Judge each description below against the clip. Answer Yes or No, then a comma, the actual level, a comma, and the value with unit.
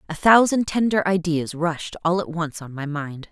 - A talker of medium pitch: Yes, medium, 170 Hz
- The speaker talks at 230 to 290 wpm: No, average, 200 wpm